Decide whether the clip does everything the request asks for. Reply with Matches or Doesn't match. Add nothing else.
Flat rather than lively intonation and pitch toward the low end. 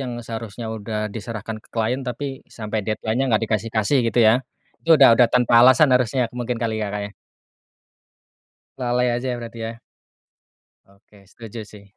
Matches